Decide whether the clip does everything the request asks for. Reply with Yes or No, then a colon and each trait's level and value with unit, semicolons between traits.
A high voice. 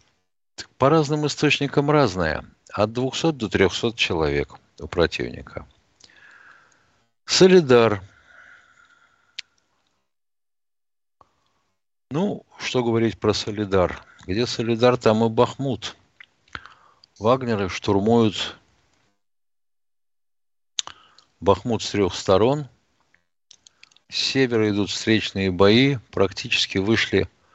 No: low, 110 Hz